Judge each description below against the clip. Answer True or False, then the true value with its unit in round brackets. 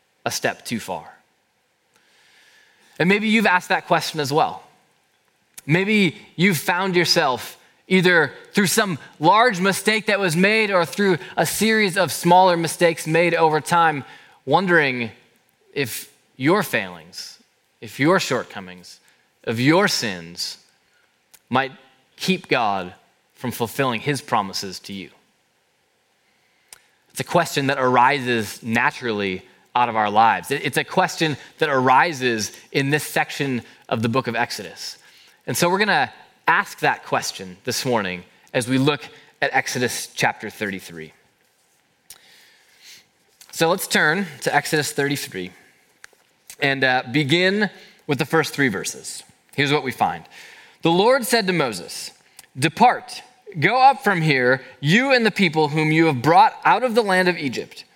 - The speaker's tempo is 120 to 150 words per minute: True (140 wpm)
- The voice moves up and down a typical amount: False (6.5 semitones)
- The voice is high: False (155 Hz)